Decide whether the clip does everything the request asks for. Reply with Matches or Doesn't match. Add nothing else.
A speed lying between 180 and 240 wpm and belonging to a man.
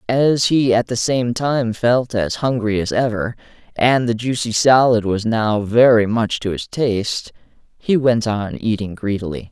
Doesn't match